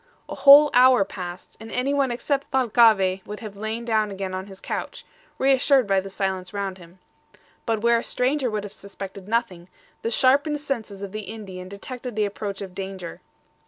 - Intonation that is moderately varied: Yes, average, 4.4 semitones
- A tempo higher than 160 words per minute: Yes, average, 180 wpm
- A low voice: No, high, 210 Hz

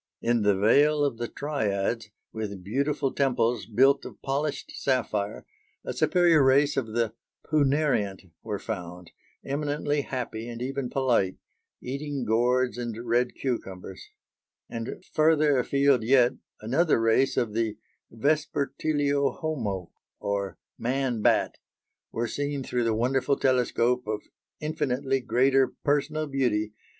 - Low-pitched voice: Yes, low, 125 Hz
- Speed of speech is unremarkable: No, slow, 120 wpm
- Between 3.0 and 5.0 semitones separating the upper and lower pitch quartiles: Yes, average, 4.0 semitones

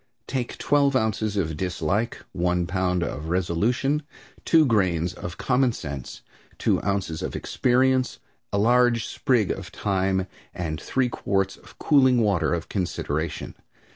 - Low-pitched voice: Yes, low, 100 Hz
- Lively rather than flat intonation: Yes, wide, 5.9 semitones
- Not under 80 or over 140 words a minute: Yes, slow, 135 wpm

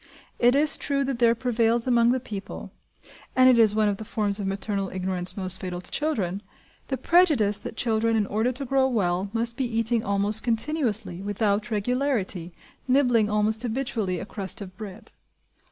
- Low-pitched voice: No, high, 220 Hz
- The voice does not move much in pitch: No, average, 3.7 semitones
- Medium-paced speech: Yes, average, 175 wpm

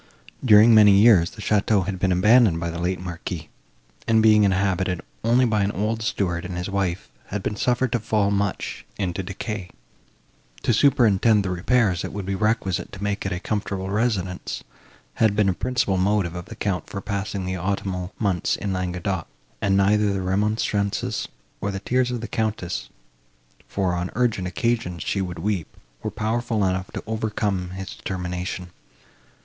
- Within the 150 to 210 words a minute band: Yes, average, 170 wpm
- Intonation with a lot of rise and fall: No, average, 2.8 semitones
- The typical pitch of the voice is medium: No, low, 100 Hz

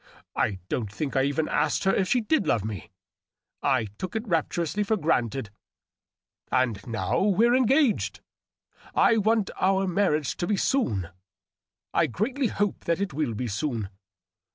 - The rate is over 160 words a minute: No, average, 155 wpm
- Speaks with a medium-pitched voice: Yes, medium, 170 Hz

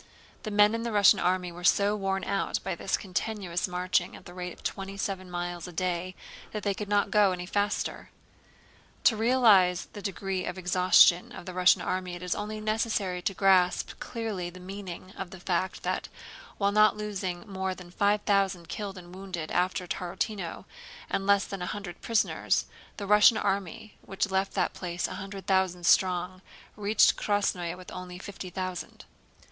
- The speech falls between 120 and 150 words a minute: No, average, 180 wpm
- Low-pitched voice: No, high, 190 Hz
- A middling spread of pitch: No, narrow, 2.1 semitones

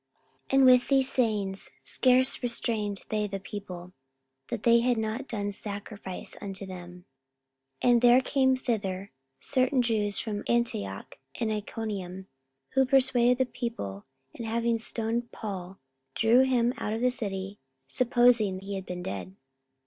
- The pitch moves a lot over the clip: No, average, 4.0 semitones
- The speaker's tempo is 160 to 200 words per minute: No, average, 145 wpm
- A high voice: Yes, high, 220 Hz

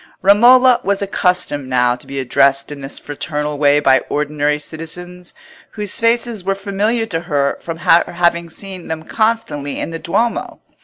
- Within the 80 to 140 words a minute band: No, average, 160 wpm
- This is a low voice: No, medium, 170 Hz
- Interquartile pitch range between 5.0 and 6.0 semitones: Yes, wide, 5.4 semitones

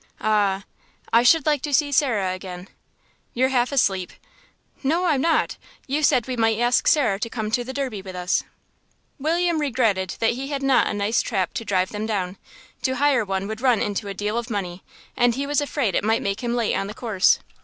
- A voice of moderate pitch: No, high, 230 Hz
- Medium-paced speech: No, fast, 210 wpm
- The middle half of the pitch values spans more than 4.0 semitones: Yes, average, 5.2 semitones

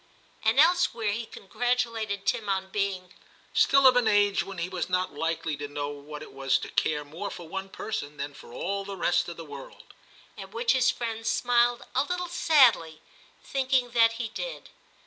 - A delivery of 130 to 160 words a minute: No, average, 195 wpm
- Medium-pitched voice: No, high, 200 Hz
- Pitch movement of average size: No, wide, 6.4 semitones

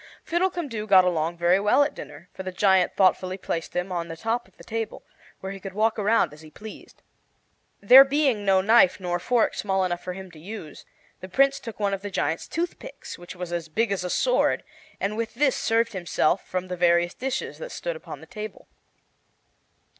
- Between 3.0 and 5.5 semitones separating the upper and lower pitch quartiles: Yes, average, 4.3 semitones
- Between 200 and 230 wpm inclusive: Yes, fast, 205 wpm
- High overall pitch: Yes, high, 195 Hz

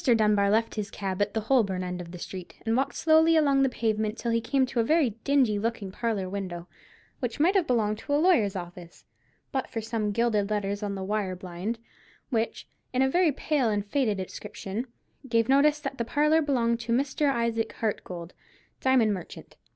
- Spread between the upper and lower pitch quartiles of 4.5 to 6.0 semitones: Yes, average, 4.9 semitones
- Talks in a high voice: Yes, high, 225 Hz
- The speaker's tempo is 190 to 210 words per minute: Yes, average, 195 wpm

